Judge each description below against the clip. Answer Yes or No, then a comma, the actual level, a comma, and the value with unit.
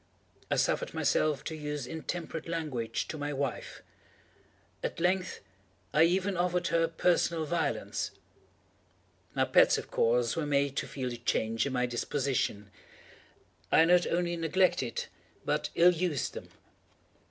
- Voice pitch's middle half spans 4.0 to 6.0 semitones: Yes, average, 4.4 semitones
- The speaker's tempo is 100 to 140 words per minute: Yes, slow, 135 wpm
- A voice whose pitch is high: No, medium, 155 Hz